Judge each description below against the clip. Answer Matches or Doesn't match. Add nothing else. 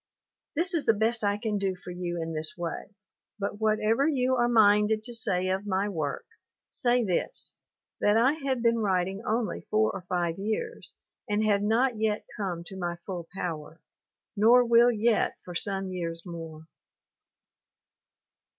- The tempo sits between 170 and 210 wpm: Doesn't match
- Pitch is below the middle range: Doesn't match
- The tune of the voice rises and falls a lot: Doesn't match